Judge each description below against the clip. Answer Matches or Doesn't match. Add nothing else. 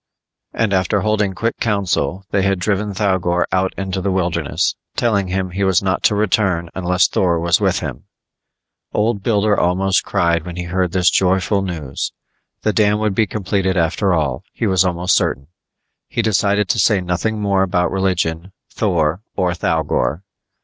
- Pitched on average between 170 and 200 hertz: Doesn't match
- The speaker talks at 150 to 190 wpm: Matches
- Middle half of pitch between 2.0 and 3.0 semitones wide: Matches